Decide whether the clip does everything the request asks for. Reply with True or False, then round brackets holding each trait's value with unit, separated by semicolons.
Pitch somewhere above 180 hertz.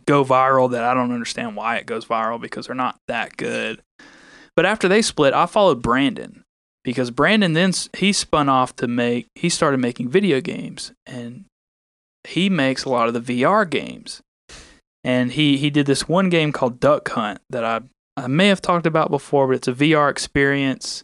False (135 Hz)